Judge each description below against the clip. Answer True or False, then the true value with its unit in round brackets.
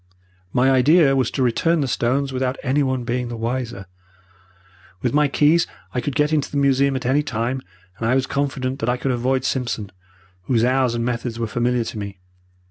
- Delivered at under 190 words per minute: False (195 wpm)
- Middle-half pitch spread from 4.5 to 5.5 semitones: False (2.5 semitones)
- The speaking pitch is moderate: False (130 Hz)